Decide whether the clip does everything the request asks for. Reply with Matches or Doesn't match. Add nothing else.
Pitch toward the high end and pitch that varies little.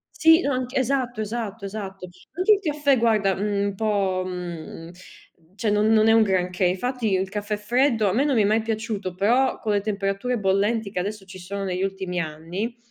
Doesn't match